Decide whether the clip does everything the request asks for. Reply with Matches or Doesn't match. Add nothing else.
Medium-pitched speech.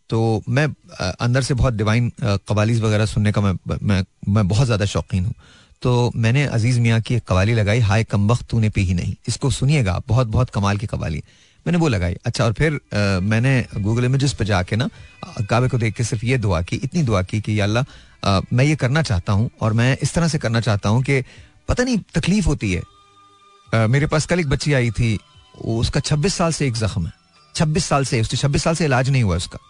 Doesn't match